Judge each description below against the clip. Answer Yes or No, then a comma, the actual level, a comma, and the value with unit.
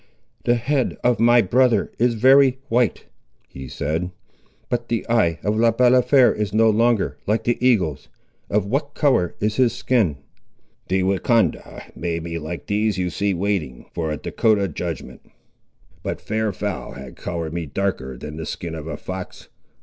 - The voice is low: Yes, low, 105 Hz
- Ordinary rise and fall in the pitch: No, wide, 5.9 semitones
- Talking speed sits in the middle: Yes, average, 165 wpm